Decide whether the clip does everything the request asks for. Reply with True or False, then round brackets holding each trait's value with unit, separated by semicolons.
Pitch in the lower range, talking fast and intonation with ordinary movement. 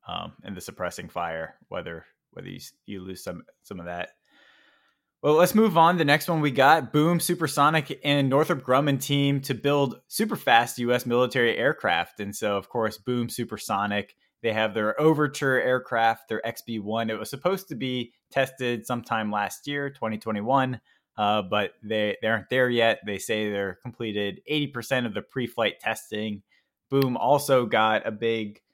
False (120 Hz; 175 wpm; 4.5 semitones)